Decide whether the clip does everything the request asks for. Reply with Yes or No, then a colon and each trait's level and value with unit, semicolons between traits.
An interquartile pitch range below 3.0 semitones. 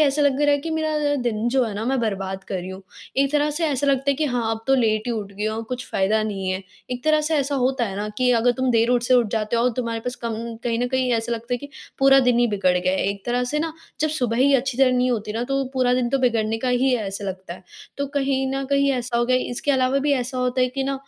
No: average, 3.3 semitones